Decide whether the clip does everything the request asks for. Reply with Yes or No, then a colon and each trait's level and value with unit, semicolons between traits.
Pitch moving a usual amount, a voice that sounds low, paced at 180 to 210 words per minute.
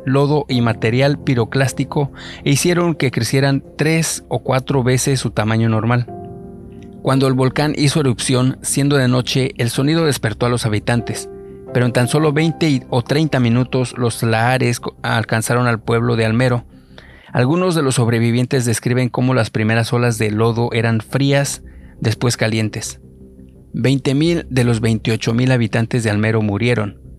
No: average, 3.2 semitones; low, 125 Hz; average, 150 wpm